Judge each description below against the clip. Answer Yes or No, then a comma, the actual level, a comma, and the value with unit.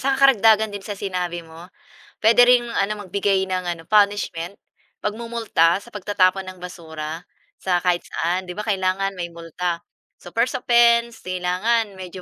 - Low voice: No, high, 190 Hz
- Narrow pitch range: No, average, 3.5 semitones